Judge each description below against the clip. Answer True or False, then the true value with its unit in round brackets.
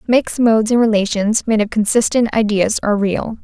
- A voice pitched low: False (215 Hz)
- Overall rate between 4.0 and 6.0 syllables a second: True (5.5 syllables/s)